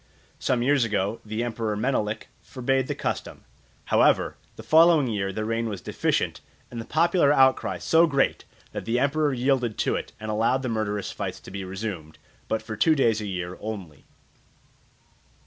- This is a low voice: Yes, low, 115 Hz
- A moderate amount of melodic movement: Yes, average, 4.1 semitones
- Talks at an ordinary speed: Yes, average, 170 wpm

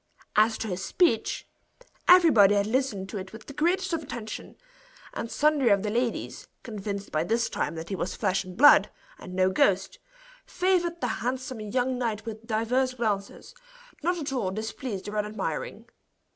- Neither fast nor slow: Yes, average, 170 wpm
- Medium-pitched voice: No, high, 220 Hz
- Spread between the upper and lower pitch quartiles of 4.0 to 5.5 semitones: Yes, average, 4.6 semitones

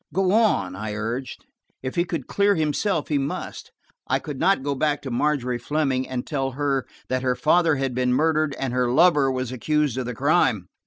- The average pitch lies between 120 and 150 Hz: Yes, low, 135 Hz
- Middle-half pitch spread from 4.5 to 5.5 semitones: No, average, 3.5 semitones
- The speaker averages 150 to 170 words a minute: No, average, 200 wpm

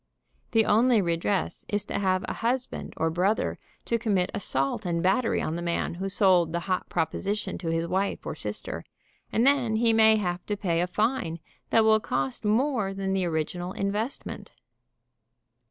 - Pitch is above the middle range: Yes, high, 195 Hz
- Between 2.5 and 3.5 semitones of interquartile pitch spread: No, average, 4.1 semitones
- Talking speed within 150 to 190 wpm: Yes, average, 170 wpm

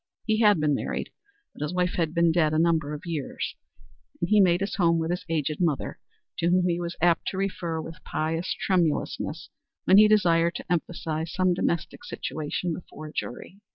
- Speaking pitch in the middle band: Yes, medium, 170 Hz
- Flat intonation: Yes, narrow, 2.2 semitones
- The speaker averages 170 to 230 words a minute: Yes, average, 190 wpm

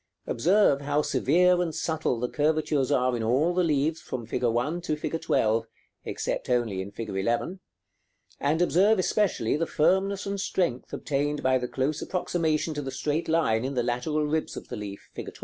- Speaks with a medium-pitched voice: Yes, medium, 150 Hz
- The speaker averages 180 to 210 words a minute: Yes, average, 185 wpm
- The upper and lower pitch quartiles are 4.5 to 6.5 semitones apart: Yes, average, 5.1 semitones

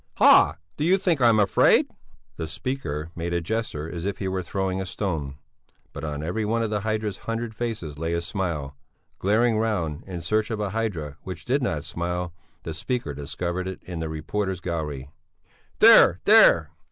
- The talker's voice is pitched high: No, very low, 90 Hz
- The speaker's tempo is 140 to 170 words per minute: No, average, 180 wpm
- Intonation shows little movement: No, average, 5.1 semitones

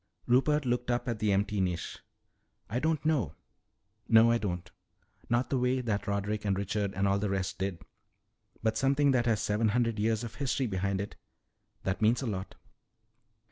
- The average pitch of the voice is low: Yes, low, 110 Hz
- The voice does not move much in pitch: No, average, 3.6 semitones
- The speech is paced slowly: No, average, 180 wpm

